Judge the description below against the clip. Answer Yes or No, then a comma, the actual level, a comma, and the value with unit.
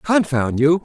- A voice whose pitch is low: No, medium, 155 Hz